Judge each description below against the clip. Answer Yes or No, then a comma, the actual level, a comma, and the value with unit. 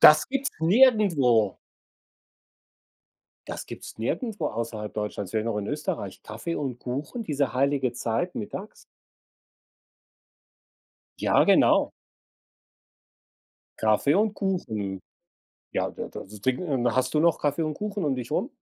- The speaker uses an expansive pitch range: Yes, wide, 7.2 semitones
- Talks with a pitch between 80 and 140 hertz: Yes, low, 135 Hz